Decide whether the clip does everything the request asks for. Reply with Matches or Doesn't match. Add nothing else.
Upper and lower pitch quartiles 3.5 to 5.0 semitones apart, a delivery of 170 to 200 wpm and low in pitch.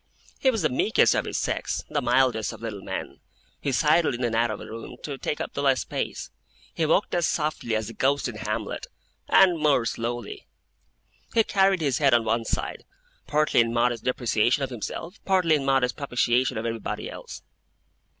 Matches